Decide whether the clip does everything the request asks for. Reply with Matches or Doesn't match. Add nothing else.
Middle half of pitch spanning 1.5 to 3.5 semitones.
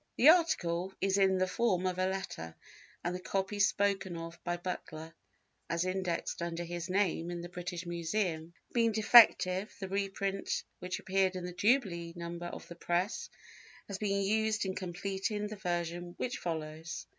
Matches